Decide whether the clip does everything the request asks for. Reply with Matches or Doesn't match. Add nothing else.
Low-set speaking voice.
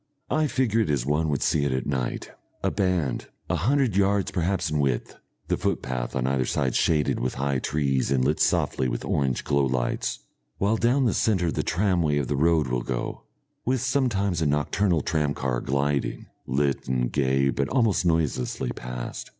Matches